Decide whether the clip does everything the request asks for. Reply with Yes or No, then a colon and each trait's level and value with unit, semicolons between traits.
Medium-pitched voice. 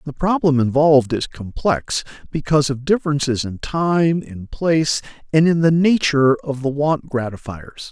Yes: medium, 145 Hz